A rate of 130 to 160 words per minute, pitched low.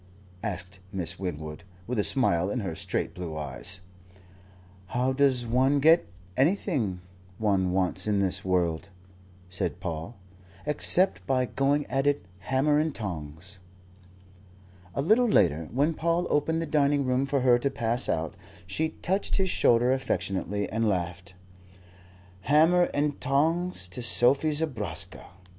Yes: slow, 135 wpm; low, 120 Hz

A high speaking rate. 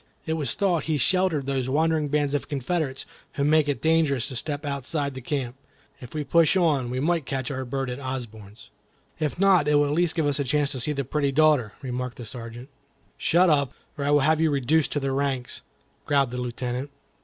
Yes: fast, 215 wpm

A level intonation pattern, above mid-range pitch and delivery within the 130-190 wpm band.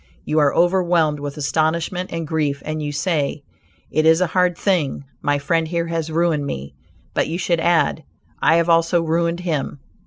No: narrow, 2.2 semitones; medium, 160 Hz; average, 180 wpm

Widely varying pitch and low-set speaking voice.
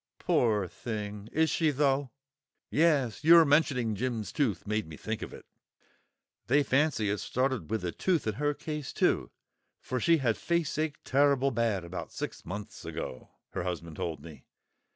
Yes: wide, 6.1 semitones; low, 125 Hz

